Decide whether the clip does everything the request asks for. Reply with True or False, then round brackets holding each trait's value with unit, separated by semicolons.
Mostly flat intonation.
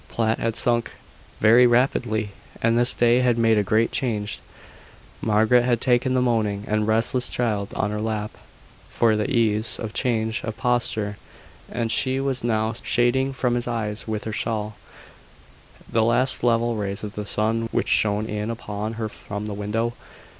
True (2.2 semitones)